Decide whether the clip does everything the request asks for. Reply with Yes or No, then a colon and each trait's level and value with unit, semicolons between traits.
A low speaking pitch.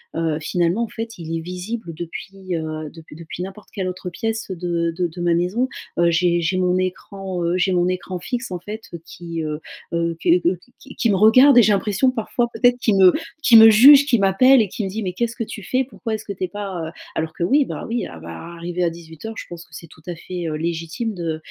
No: medium, 180 Hz